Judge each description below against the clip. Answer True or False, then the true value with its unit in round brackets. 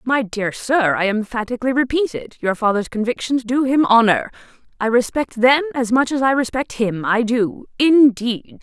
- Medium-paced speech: True (175 wpm)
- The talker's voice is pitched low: False (245 Hz)